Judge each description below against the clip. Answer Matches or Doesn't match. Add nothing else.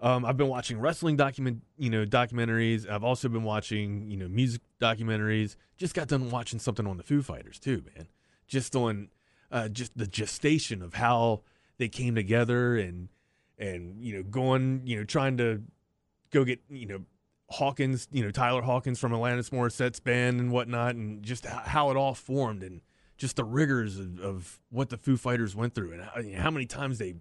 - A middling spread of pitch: Matches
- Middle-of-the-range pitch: Doesn't match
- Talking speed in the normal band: Matches